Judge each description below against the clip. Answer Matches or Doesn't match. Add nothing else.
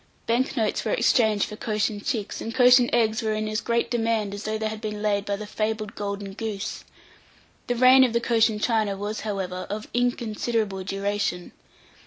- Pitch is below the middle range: Doesn't match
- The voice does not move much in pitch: Matches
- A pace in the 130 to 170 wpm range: Doesn't match